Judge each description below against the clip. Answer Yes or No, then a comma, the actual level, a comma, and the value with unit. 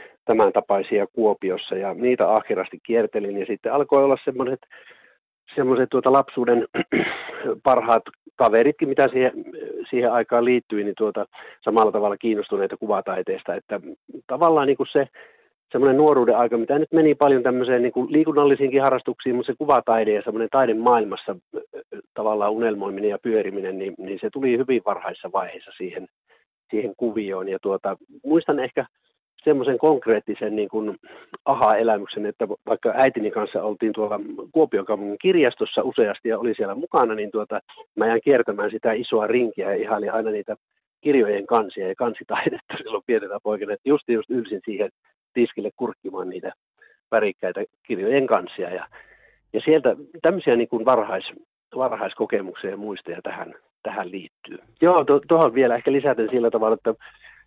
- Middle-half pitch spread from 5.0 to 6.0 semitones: Yes, wide, 5.4 semitones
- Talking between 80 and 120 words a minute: No, average, 145 wpm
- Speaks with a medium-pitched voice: No, low, 125 Hz